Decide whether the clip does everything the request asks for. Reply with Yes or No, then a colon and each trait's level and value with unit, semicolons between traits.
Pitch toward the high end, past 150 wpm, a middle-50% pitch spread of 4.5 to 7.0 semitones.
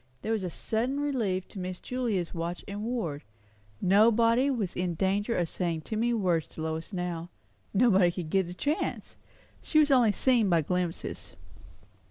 Yes: high, 195 Hz; average, 170 wpm; average, 4.8 semitones